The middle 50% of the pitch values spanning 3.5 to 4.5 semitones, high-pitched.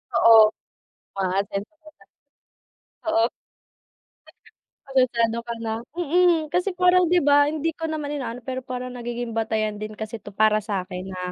No: wide, 5.6 semitones; high, 235 Hz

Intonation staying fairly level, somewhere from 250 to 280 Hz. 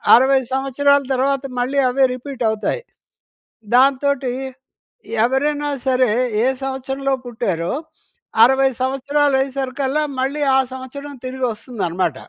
Yes: narrow, 1.7 semitones; very high, 265 Hz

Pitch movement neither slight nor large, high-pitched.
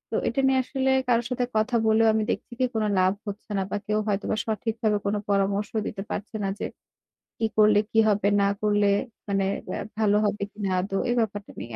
No: narrow, 1.9 semitones; high, 210 Hz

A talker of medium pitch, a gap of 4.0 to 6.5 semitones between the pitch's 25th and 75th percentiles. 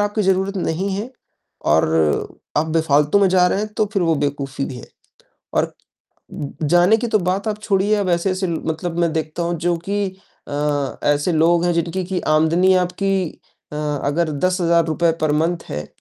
No: medium, 170 Hz; average, 3.6 semitones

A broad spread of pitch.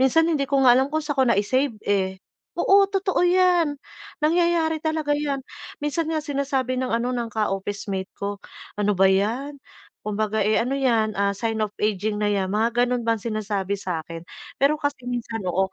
Yes: wide, 6.0 semitones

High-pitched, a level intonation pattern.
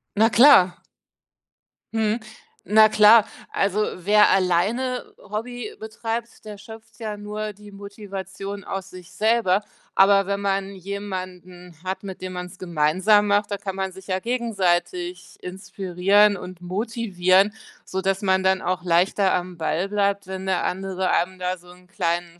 Yes: high, 195 Hz; narrow, 2.3 semitones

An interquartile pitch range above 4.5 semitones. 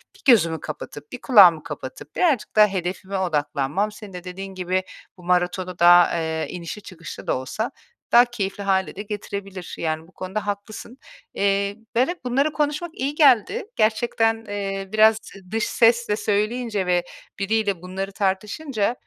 No: average, 3.7 semitones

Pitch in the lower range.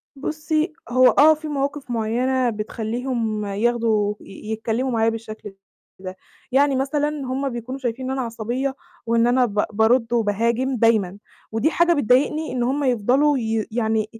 No: high, 240 Hz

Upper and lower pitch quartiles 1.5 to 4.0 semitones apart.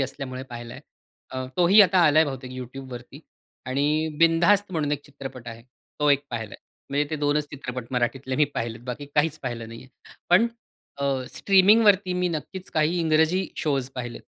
No: average, 4.4 semitones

